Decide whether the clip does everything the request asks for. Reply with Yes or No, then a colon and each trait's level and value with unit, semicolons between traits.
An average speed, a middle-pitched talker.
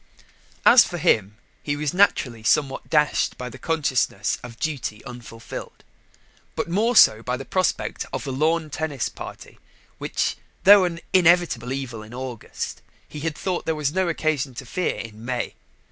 Yes: average, 160 wpm; medium, 145 Hz